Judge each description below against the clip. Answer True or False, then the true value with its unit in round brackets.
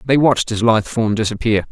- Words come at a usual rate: False (210 wpm)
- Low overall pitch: True (115 Hz)